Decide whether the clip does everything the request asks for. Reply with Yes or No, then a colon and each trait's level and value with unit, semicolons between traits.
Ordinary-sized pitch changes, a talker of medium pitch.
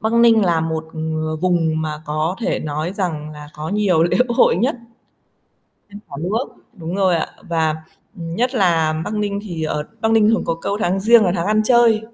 Yes: average, 5.0 semitones; medium, 175 Hz